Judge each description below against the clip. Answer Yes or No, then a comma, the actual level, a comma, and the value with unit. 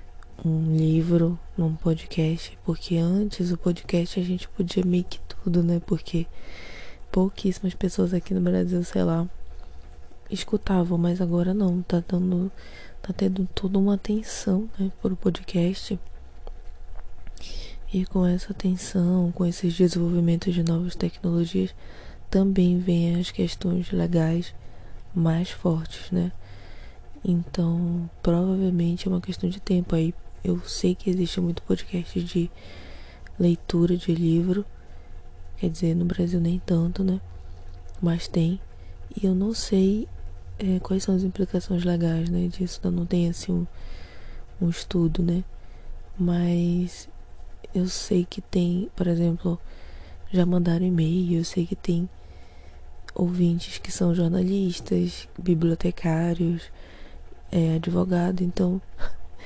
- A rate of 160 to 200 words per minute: No, average, 125 wpm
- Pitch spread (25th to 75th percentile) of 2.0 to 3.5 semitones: Yes, narrow, 2.5 semitones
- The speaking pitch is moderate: Yes, medium, 175 Hz